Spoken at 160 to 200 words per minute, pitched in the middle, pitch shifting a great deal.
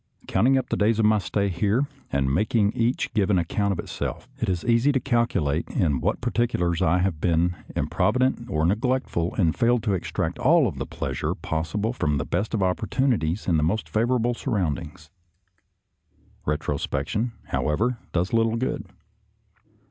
No: average, 170 wpm; low, 100 Hz; wide, 5.8 semitones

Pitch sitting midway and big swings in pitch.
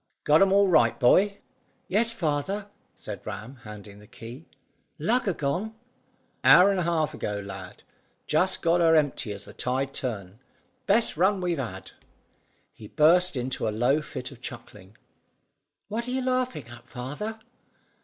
Yes: medium, 150 Hz; wide, 8.4 semitones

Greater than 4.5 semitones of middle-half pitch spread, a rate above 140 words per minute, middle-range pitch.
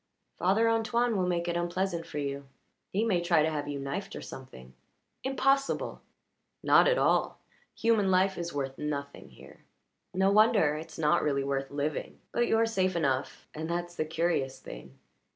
Yes: wide, 5.5 semitones; average, 170 wpm; medium, 170 Hz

